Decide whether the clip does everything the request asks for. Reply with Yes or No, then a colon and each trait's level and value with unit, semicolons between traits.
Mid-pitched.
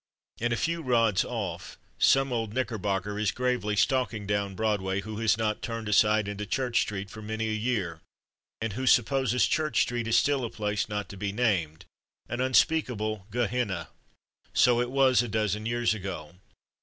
No: low, 110 Hz